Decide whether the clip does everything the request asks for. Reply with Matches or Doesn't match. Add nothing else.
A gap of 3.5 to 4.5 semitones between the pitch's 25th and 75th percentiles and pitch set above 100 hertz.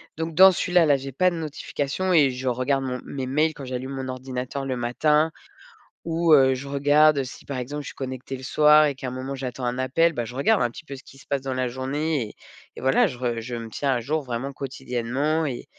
Doesn't match